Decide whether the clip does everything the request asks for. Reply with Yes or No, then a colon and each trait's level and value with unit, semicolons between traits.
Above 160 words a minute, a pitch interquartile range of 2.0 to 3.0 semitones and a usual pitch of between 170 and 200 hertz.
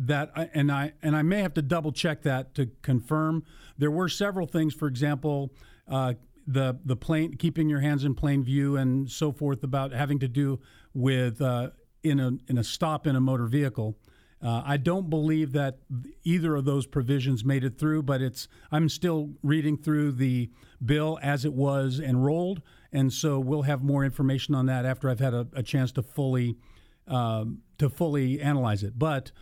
No: average, 190 wpm; narrow, 2.6 semitones; medium, 140 Hz